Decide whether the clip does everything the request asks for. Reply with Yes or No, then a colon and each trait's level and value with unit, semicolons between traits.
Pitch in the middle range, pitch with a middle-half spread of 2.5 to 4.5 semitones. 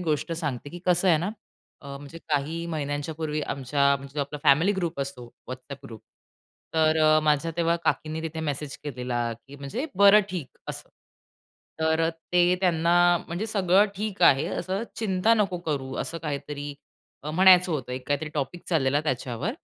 Yes: medium, 155 Hz; average, 3.8 semitones